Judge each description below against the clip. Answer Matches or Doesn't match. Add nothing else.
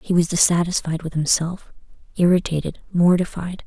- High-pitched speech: Doesn't match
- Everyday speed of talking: Doesn't match